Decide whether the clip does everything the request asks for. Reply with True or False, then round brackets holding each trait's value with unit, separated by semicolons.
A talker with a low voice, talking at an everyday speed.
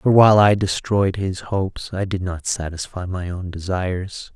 True (95 Hz; 180 wpm)